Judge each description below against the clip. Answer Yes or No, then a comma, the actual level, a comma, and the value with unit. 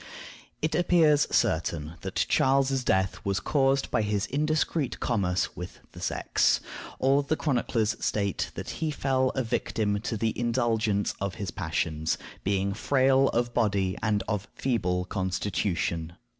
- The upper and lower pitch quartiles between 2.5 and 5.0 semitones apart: No, wide, 5.6 semitones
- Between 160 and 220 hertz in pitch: No, low, 110 Hz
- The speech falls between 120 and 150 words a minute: Yes, average, 140 wpm